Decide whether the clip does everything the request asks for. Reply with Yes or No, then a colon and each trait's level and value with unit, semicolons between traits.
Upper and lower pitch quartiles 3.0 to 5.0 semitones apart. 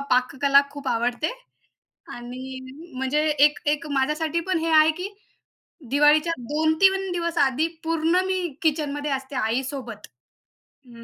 Yes: average, 3.3 semitones